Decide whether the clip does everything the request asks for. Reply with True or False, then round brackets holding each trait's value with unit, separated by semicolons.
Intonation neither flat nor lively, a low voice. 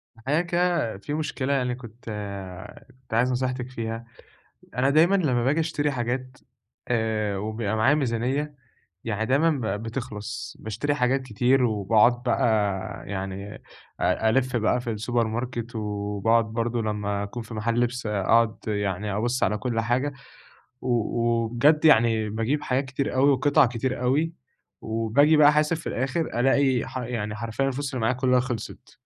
True (3.3 semitones; 120 Hz)